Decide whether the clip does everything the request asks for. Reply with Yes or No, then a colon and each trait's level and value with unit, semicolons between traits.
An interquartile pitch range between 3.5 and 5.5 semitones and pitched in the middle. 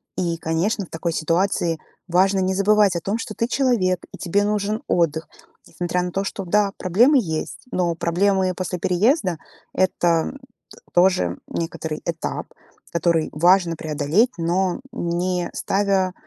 No: average, 2.8 semitones; medium, 180 Hz